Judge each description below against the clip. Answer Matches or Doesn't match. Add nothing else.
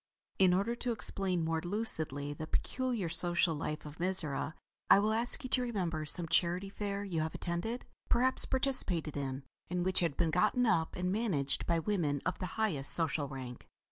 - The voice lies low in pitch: Doesn't match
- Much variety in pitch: Doesn't match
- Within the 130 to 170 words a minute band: Doesn't match